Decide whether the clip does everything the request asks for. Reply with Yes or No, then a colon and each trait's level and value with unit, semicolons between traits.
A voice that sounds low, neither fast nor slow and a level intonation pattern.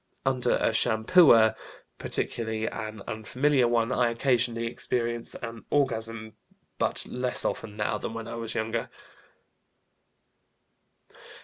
No: low, 115 Hz; slow, 110 wpm; narrow, 1.8 semitones